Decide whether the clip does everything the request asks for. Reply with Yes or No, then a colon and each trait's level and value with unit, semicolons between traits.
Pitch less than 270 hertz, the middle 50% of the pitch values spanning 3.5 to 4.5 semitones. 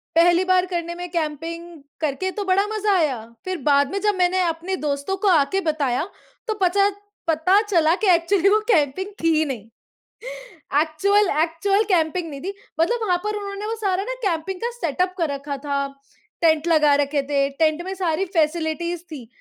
No: very high, 340 Hz; average, 3.9 semitones